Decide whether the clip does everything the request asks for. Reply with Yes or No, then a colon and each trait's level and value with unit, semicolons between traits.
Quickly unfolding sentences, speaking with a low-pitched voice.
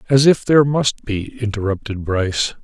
No: average, 160 wpm; low, 115 Hz